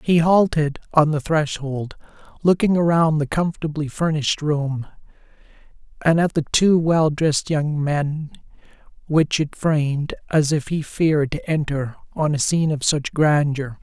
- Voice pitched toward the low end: No, medium, 150 Hz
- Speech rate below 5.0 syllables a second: Yes, 4.4 syllables/s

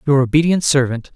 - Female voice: No, male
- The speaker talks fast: No, average, 155 wpm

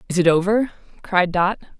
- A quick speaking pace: No, average, 165 wpm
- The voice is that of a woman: Yes, female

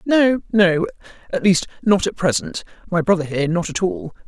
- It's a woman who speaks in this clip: Yes, female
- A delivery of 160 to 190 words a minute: Yes, average, 170 wpm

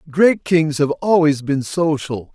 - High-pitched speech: No, medium, 150 Hz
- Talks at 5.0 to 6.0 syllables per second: No, 3.7 syllables/s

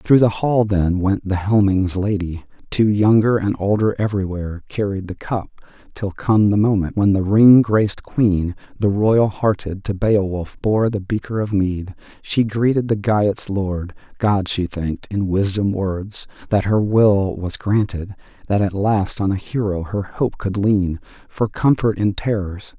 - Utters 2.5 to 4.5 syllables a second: Yes, 4.2 syllables/s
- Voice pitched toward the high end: No, low, 100 Hz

